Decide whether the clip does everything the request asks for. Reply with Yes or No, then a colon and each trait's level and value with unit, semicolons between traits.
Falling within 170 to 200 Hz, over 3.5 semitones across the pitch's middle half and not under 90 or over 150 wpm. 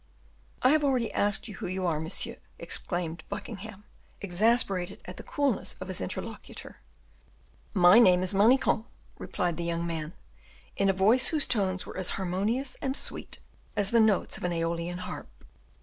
No: high, 190 Hz; average, 4.3 semitones; average, 165 wpm